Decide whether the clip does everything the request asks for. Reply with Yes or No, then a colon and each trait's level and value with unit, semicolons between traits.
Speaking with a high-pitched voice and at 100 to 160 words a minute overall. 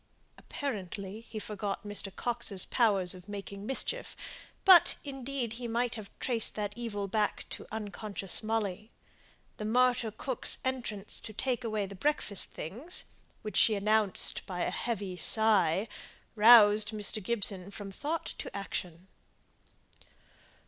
Yes: high, 215 Hz; slow, 135 wpm